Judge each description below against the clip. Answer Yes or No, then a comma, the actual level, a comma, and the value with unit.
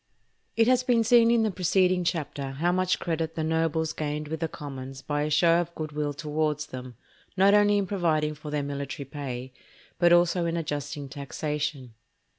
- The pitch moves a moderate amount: Yes, average, 3.3 semitones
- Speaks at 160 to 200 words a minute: Yes, average, 185 wpm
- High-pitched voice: No, medium, 155 Hz